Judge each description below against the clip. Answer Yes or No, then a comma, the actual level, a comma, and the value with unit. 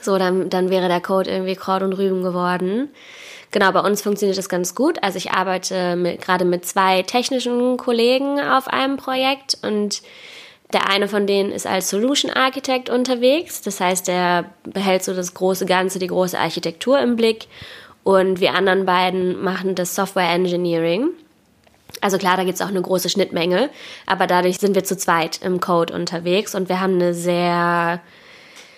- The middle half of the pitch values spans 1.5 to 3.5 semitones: No, average, 4.3 semitones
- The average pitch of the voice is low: No, high, 190 Hz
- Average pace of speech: Yes, average, 175 wpm